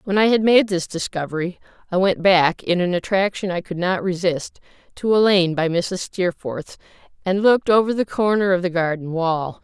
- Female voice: Yes, female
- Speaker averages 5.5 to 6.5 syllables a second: No, 5.0 syllables/s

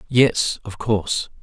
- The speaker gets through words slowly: Yes, slow, 125 wpm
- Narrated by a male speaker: Yes, male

